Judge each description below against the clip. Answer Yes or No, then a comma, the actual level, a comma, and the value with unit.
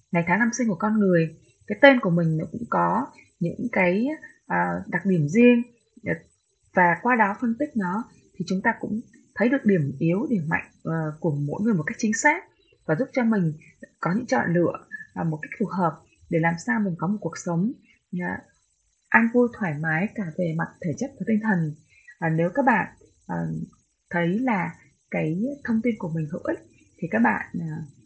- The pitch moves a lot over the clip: Yes, wide, 6.0 semitones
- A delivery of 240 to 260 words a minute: No, average, 190 wpm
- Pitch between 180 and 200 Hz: Yes, high, 190 Hz